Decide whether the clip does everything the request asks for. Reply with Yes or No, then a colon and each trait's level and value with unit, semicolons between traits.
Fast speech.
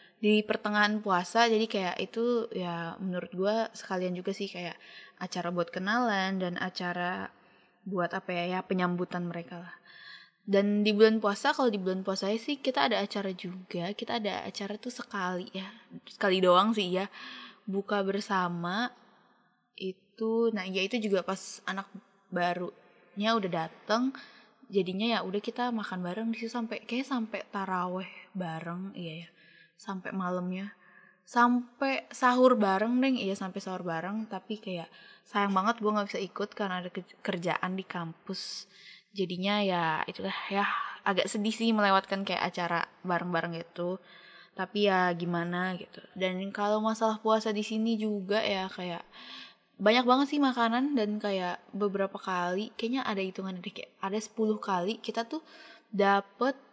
Yes: fast, 150 wpm